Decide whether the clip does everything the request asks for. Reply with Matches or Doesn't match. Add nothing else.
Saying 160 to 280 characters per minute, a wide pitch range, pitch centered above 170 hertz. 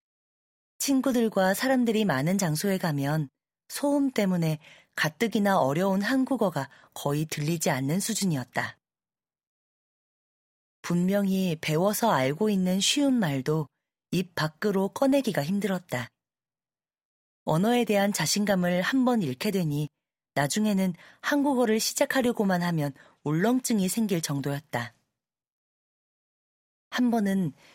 Matches